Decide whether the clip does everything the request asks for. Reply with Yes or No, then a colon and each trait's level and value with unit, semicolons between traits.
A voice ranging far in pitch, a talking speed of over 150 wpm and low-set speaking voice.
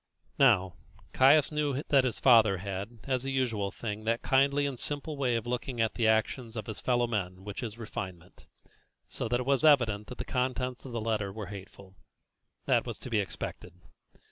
No: average, 4.0 semitones; average, 195 wpm; low, 115 Hz